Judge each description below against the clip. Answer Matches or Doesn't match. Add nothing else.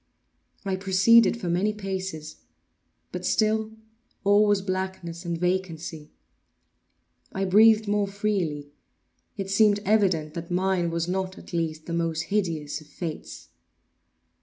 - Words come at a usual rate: Doesn't match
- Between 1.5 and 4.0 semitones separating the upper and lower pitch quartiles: Matches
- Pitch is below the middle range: Doesn't match